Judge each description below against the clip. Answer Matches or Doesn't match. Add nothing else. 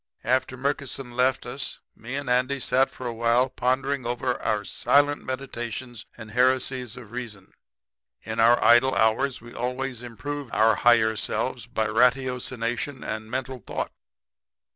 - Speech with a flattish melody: Matches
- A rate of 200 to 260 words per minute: Doesn't match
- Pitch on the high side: Doesn't match